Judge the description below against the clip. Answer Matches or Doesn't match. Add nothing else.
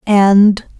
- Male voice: Doesn't match